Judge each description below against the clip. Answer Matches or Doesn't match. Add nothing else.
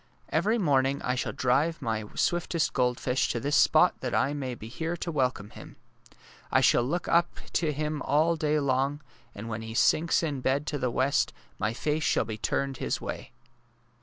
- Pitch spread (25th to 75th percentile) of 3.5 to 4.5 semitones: Matches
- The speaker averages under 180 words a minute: Doesn't match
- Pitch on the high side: Doesn't match